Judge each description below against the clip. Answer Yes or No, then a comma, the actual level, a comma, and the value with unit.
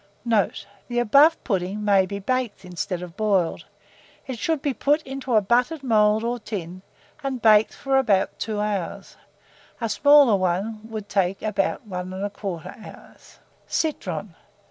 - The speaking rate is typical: Yes, average, 145 wpm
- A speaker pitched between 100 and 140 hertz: No, high, 215 Hz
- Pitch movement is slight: No, average, 4.6 semitones